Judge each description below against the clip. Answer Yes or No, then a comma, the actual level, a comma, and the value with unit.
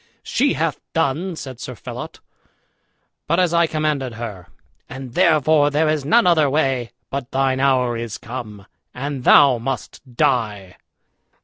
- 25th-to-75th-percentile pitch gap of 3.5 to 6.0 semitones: Yes, average, 4.2 semitones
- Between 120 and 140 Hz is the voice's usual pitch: Yes, low, 135 Hz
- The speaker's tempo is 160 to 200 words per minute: No, average, 140 wpm